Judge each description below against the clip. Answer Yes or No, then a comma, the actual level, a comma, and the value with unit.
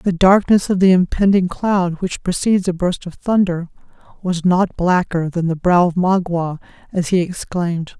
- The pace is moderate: Yes, average, 175 wpm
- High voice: No, medium, 180 Hz